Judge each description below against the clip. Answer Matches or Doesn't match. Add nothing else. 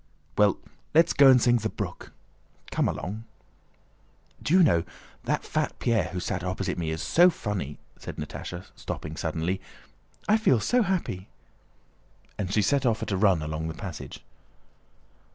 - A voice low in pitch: Matches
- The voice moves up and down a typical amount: Doesn't match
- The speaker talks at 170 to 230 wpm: Doesn't match